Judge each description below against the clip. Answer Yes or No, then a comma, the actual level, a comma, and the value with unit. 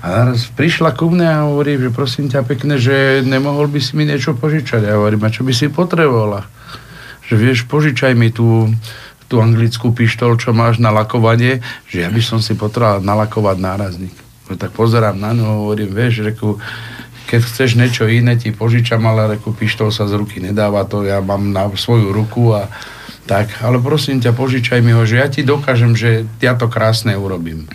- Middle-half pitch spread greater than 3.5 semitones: No, average, 3.2 semitones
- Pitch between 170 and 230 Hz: No, low, 115 Hz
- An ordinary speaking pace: Yes, average, 190 wpm